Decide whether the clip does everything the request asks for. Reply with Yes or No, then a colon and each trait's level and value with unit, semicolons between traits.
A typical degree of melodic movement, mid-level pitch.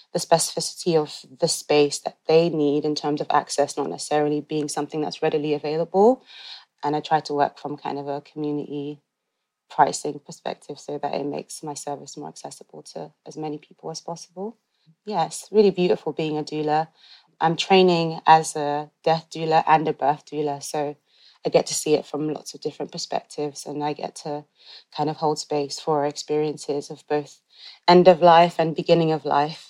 No: narrow, 1.7 semitones; medium, 150 Hz